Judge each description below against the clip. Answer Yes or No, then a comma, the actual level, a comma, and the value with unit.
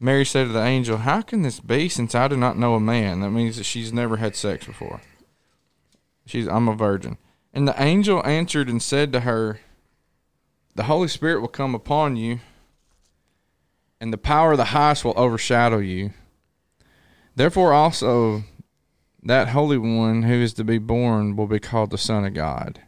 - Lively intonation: No, average, 4.0 semitones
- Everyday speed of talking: Yes, average, 180 wpm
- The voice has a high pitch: No, low, 120 Hz